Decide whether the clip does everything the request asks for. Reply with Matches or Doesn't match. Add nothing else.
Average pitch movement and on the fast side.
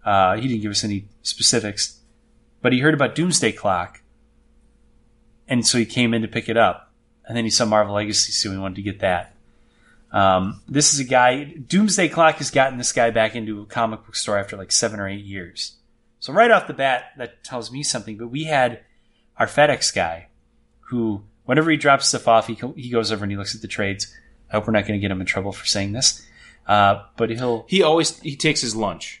Matches